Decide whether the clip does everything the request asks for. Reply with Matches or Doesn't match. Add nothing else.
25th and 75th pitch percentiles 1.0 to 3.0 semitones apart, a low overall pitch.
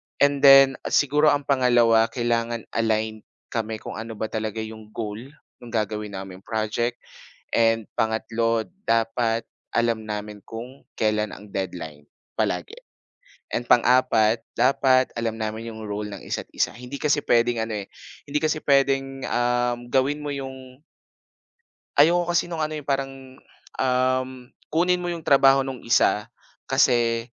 Doesn't match